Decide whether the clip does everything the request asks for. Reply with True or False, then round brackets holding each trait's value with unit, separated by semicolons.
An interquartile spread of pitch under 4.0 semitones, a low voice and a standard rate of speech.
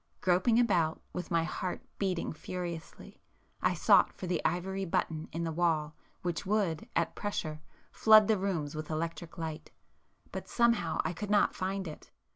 False (3.3 semitones; 175 Hz; 160 wpm)